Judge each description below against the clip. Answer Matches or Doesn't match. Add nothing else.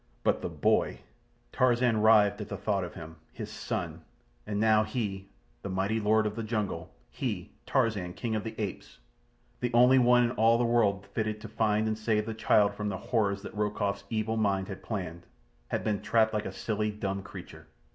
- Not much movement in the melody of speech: Matches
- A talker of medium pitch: Doesn't match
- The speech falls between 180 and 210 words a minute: Matches